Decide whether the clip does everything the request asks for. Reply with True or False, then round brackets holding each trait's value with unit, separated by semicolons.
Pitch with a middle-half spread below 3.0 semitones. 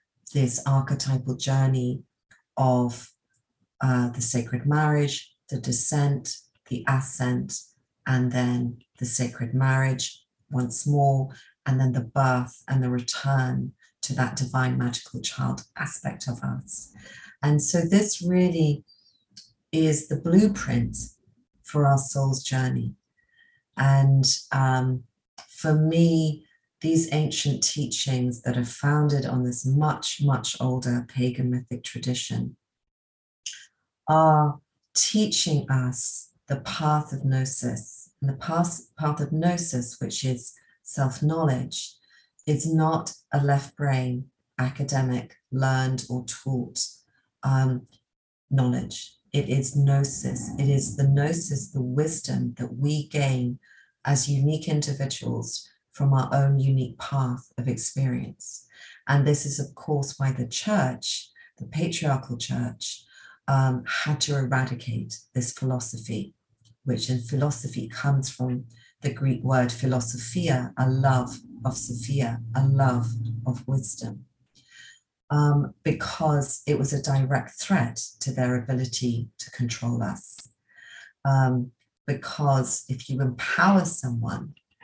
True (2.6 semitones)